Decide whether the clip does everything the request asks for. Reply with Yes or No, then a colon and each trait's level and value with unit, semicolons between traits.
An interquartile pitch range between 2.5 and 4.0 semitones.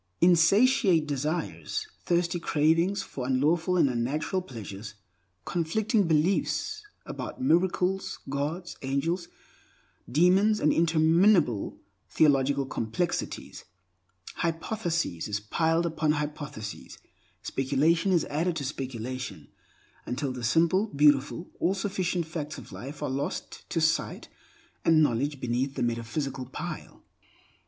No: average, 4.7 semitones